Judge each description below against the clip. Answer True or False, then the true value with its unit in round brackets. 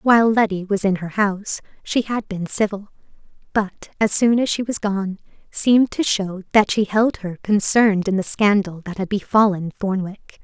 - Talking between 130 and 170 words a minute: False (185 wpm)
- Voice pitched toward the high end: True (205 Hz)